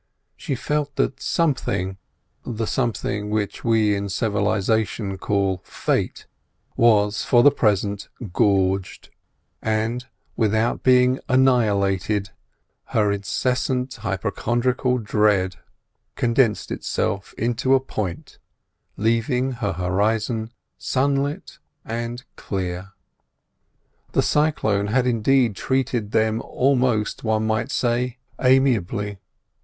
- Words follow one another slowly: Yes, slow, 90 wpm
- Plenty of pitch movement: No, average, 3.6 semitones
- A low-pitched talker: Yes, low, 110 Hz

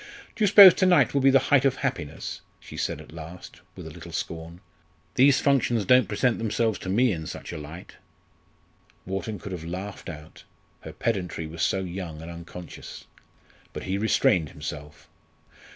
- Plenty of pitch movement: Yes, wide, 7.3 semitones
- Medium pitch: No, very low, 95 Hz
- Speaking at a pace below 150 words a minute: No, average, 175 wpm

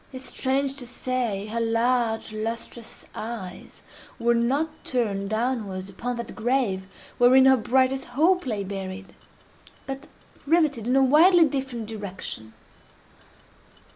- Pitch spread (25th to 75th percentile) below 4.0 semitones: Yes, average, 3.6 semitones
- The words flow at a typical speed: No, slow, 105 wpm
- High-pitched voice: Yes, high, 240 Hz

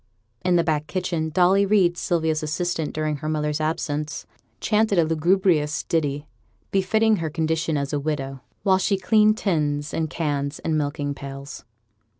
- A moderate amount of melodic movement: Yes, average, 3.5 semitones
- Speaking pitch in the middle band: Yes, medium, 160 Hz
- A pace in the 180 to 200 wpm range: No, average, 155 wpm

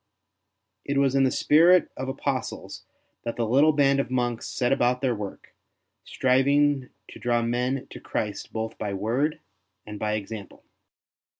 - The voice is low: Yes, low, 125 Hz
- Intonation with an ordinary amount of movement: Yes, average, 3.4 semitones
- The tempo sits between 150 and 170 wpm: Yes, average, 155 wpm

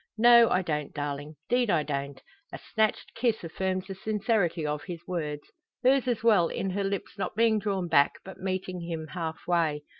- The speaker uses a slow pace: No, average, 180 wpm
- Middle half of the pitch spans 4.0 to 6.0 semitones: Yes, average, 5.2 semitones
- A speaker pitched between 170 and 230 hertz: Yes, medium, 185 Hz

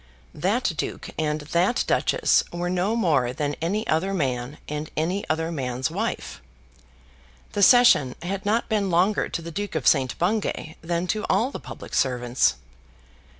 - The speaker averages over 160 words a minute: No, average, 155 wpm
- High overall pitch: No, medium, 170 Hz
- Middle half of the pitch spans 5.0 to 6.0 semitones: Yes, wide, 5.4 semitones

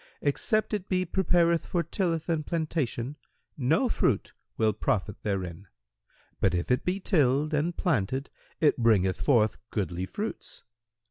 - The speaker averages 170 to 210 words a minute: No, slow, 135 wpm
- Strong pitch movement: Yes, wide, 8.0 semitones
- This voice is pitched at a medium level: Yes, medium, 145 Hz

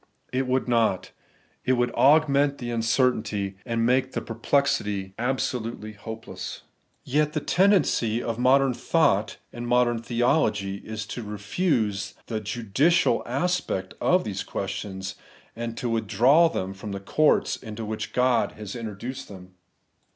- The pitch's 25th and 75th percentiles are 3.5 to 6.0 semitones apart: Yes, average, 3.8 semitones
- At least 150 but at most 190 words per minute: No, slow, 135 wpm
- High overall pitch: No, low, 115 Hz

